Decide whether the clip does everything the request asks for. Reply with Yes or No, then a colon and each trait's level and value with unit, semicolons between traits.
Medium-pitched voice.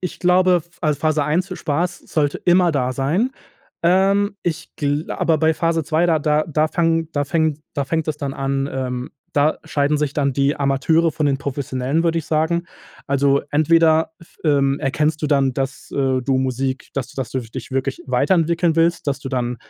Yes: medium, 150 Hz